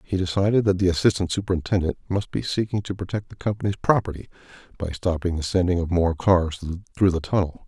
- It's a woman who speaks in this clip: No, male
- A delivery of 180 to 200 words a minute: Yes, average, 190 wpm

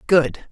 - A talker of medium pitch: Yes, medium, 145 Hz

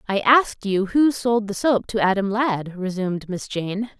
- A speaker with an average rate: Yes, average, 195 wpm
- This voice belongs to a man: No, female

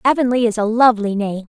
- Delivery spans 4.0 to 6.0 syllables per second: No, 6.6 syllables/s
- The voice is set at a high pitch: Yes, high, 225 Hz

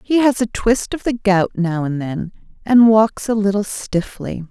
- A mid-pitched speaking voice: No, high, 205 Hz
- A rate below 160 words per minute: No, average, 200 wpm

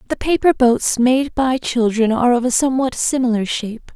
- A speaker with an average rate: Yes, average, 180 wpm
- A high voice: Yes, high, 245 Hz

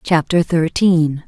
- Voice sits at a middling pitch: Yes, medium, 165 Hz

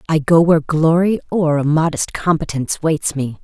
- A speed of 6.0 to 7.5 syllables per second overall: No, 5.1 syllables/s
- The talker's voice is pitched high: No, medium, 160 Hz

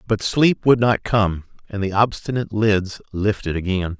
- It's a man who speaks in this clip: Yes, male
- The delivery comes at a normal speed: Yes, average, 165 wpm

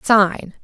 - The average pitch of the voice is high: Yes, high, 195 Hz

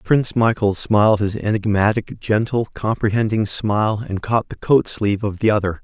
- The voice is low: Yes, low, 105 Hz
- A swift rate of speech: No, average, 165 wpm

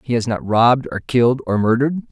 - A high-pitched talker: No, low, 125 Hz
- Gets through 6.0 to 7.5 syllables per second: Yes, 6.5 syllables/s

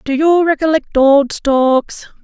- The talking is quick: No, slow, 135 wpm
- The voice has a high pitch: Yes, very high, 290 Hz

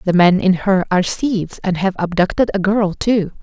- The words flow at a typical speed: No, fast, 210 wpm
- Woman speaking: Yes, female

